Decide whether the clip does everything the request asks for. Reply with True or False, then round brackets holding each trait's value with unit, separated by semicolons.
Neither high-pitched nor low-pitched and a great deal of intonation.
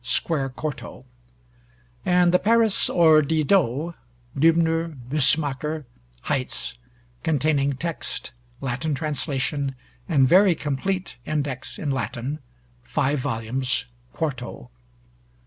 False (150 Hz; 3.4 semitones)